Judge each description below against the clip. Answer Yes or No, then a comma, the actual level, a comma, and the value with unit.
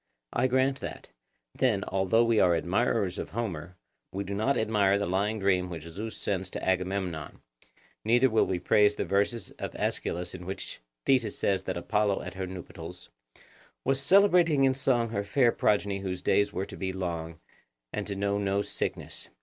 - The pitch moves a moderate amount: Yes, average, 3.5 semitones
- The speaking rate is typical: Yes, average, 175 wpm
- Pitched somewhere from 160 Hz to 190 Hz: No, low, 100 Hz